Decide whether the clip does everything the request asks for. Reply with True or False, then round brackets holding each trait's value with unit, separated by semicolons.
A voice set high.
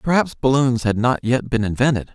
False (125 Hz)